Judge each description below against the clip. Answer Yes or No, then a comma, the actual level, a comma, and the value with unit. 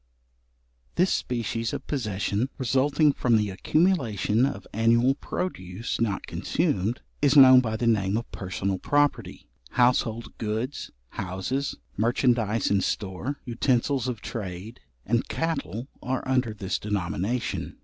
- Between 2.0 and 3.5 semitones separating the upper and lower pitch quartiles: No, average, 4.3 semitones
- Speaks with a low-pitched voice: Yes, low, 115 Hz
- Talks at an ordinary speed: No, slow, 120 wpm